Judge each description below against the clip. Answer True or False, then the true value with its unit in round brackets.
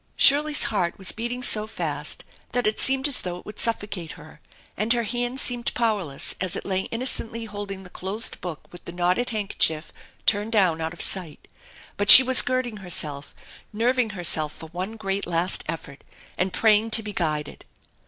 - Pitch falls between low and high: False (205 Hz)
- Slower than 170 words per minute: False (180 wpm)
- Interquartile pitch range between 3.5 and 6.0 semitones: True (4.7 semitones)